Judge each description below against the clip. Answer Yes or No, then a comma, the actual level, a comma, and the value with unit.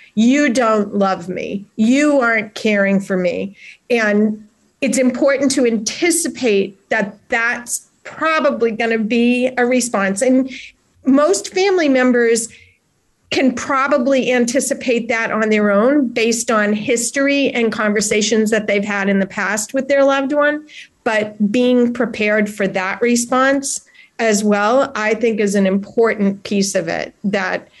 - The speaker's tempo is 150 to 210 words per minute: No, average, 140 wpm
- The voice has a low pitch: No, high, 230 Hz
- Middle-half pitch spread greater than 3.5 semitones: Yes, average, 3.9 semitones